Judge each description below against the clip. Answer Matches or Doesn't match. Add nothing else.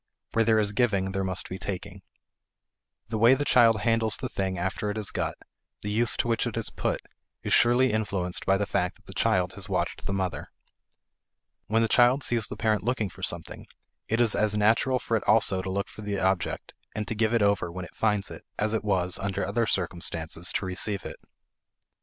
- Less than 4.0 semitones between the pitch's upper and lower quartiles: Matches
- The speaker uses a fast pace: Matches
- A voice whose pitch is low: Matches